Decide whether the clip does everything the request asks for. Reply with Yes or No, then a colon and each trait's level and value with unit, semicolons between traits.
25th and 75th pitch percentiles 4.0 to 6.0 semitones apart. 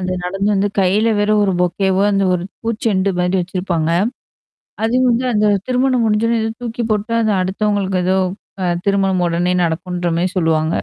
No: average, 3.3 semitones